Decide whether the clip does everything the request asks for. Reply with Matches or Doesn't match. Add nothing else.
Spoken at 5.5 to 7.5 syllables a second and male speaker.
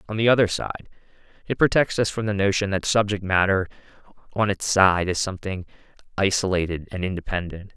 Matches